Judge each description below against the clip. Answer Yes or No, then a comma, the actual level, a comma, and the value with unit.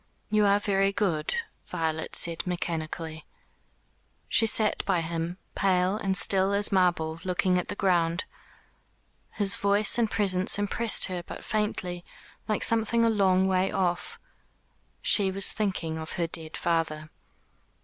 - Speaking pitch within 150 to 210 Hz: Yes, medium, 185 Hz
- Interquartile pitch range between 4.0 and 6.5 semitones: No, average, 3.3 semitones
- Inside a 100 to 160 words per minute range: Yes, average, 140 wpm